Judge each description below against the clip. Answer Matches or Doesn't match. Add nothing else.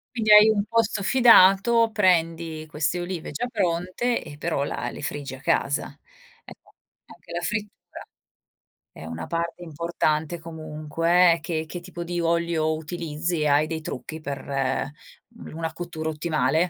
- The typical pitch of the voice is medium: Matches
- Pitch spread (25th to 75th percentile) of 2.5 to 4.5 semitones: Matches